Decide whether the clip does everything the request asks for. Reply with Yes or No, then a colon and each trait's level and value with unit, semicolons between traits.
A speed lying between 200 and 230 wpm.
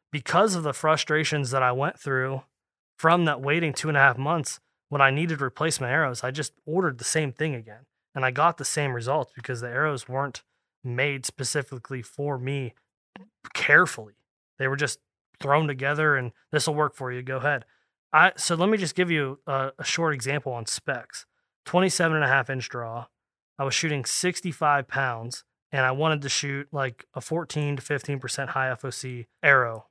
No: average, 185 wpm